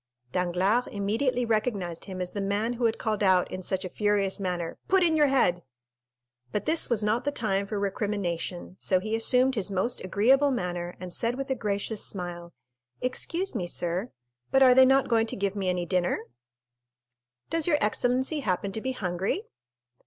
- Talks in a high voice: Yes, high, 210 Hz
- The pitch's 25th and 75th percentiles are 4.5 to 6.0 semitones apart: Yes, average, 5.3 semitones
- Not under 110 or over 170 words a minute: No, average, 180 wpm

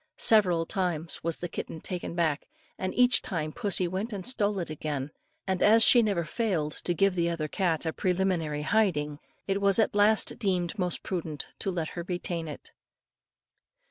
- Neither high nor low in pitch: Yes, medium, 180 Hz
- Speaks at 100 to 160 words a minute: No, average, 175 wpm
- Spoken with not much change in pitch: No, average, 3.5 semitones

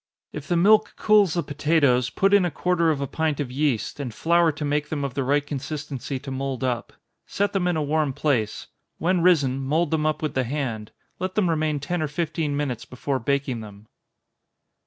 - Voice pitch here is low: No, medium, 145 Hz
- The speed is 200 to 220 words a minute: Yes, fast, 205 wpm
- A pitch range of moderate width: Yes, average, 3.7 semitones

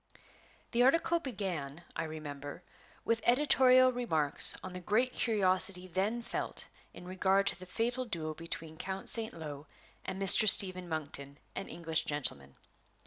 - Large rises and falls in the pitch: Yes, wide, 6.3 semitones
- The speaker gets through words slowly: No, average, 145 wpm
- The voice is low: No, medium, 185 Hz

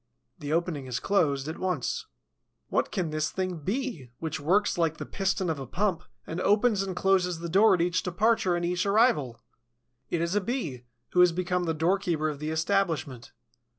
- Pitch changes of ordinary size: Yes, average, 3.8 semitones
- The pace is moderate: Yes, average, 185 wpm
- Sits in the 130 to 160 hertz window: No, medium, 175 Hz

